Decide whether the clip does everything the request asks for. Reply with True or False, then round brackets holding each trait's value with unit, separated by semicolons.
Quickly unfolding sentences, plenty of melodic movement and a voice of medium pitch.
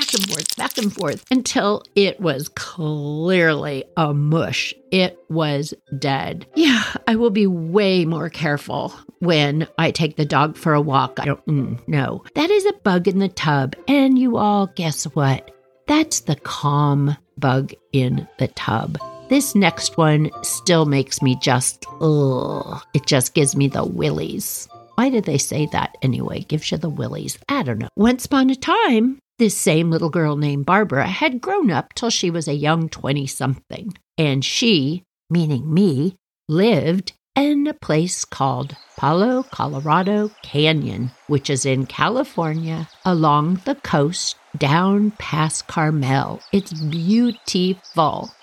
False (150 wpm; 5.8 semitones; 160 Hz)